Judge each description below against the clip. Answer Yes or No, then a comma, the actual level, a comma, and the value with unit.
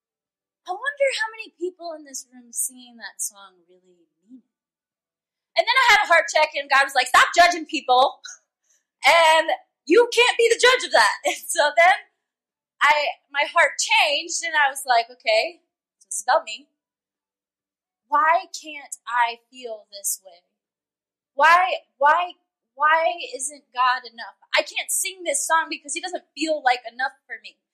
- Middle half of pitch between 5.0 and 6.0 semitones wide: Yes, wide, 5.4 semitones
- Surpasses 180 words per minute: No, average, 165 wpm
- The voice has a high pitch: Yes, very high, 300 Hz